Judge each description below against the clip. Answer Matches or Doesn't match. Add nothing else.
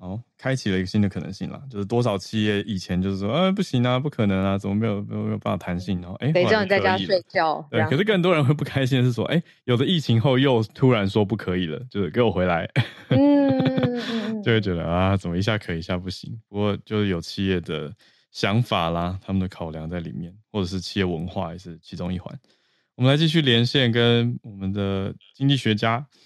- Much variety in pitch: Matches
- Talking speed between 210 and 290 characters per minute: Doesn't match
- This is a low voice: Matches